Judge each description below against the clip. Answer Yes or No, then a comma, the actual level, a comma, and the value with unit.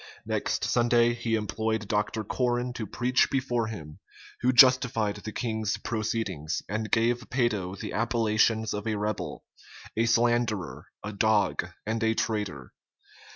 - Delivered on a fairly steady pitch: Yes, narrow, 2.0 semitones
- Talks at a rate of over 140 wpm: No, slow, 135 wpm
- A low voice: Yes, low, 110 Hz